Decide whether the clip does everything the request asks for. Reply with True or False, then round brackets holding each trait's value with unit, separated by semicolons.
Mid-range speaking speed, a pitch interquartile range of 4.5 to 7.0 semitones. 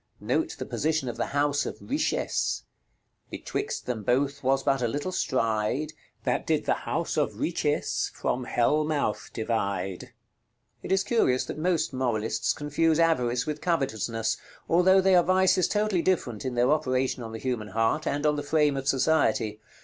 True (165 wpm; 5.1 semitones)